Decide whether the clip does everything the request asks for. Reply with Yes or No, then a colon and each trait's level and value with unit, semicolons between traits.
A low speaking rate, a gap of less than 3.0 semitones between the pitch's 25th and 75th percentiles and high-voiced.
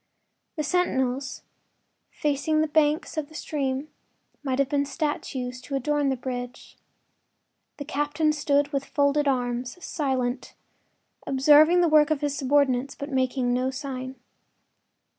Yes: slow, 130 wpm; narrow, 2.4 semitones; very high, 280 Hz